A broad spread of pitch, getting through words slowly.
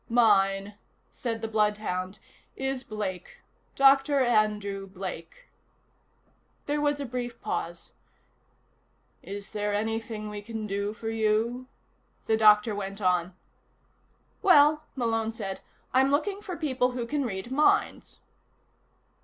No: average, 4.0 semitones; slow, 115 wpm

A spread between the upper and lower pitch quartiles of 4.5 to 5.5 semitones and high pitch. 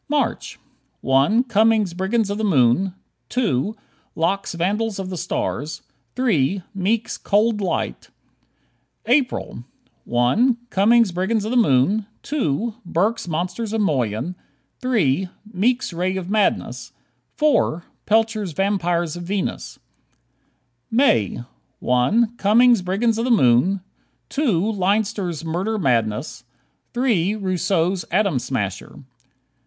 Yes: average, 4.9 semitones; high, 195 Hz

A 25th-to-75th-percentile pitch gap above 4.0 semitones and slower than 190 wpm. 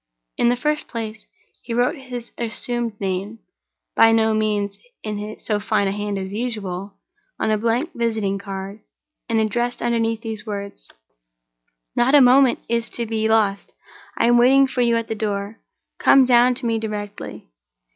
No: narrow, 2.6 semitones; average, 160 wpm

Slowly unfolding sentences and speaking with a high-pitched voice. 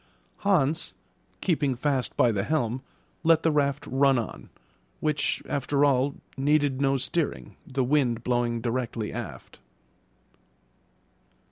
No: slow, 115 wpm; low, 135 Hz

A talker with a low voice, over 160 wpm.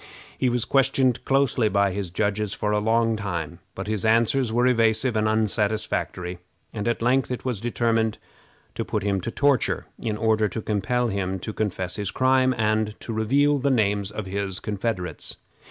Yes: low, 110 Hz; average, 175 wpm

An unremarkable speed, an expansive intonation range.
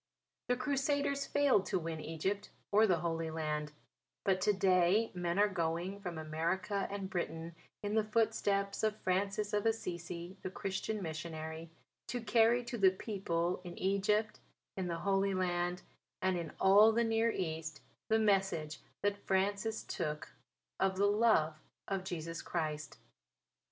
No: average, 145 wpm; average, 3.7 semitones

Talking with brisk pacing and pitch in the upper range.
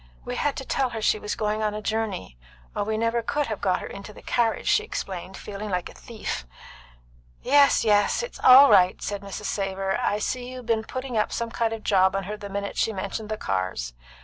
Yes: fast, 220 wpm; high, 215 Hz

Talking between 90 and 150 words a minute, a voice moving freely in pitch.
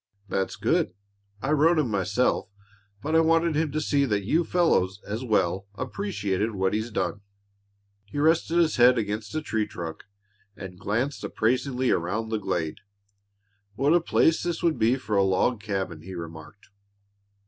No: average, 160 wpm; wide, 7.6 semitones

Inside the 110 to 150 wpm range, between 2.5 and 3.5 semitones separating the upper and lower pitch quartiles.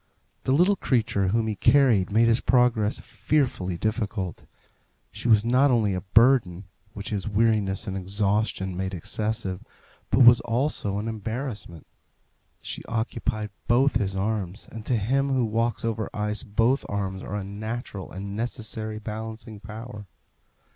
Yes: average, 145 wpm; average, 2.9 semitones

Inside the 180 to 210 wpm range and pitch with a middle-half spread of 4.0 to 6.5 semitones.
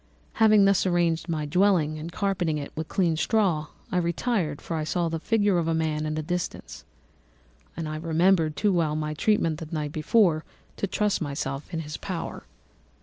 No: average, 185 wpm; average, 3.4 semitones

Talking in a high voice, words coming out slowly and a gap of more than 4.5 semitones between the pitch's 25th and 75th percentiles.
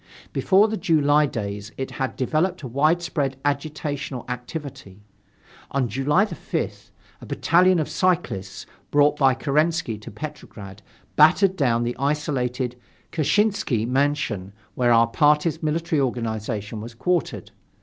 No: medium, 140 Hz; slow, 120 wpm; average, 4.9 semitones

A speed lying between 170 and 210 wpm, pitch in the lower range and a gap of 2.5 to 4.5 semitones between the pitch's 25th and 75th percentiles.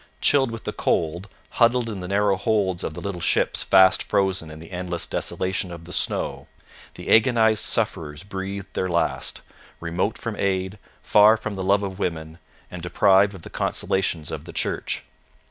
Yes: average, 175 wpm; very low, 95 Hz; average, 2.8 semitones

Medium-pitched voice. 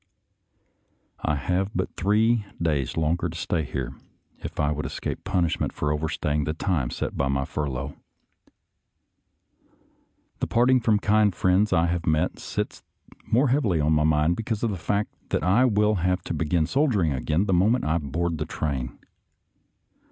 No: very low, 85 Hz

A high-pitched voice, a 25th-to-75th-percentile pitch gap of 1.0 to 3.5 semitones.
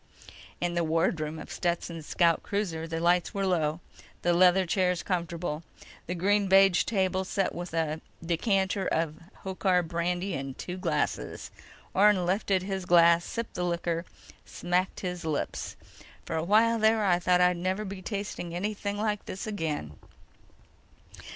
No: medium, 180 Hz; narrow, 2.4 semitones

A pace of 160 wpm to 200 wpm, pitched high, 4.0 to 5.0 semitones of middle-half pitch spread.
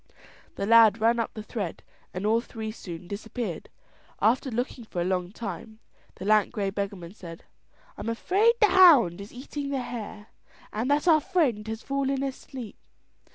Yes: average, 170 wpm; high, 225 Hz; average, 4.6 semitones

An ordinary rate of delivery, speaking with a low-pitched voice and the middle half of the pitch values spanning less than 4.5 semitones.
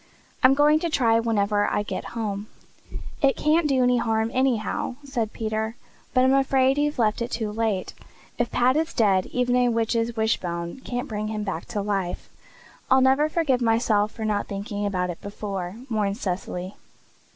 No: average, 175 wpm; high, 225 Hz; average, 3.8 semitones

